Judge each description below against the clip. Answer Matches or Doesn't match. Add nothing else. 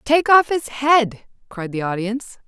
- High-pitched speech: Matches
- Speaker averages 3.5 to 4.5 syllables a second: Matches